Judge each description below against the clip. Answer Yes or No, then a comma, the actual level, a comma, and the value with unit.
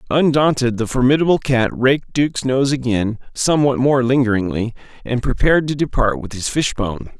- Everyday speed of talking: Yes, average, 150 wpm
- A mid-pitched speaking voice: No, low, 130 Hz